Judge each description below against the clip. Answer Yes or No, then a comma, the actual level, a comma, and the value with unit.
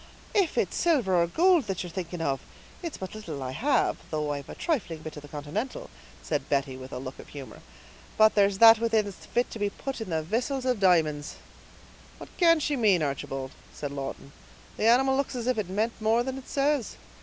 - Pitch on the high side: Yes, high, 205 Hz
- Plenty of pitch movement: Yes, wide, 8.7 semitones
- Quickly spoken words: Yes, fast, 210 wpm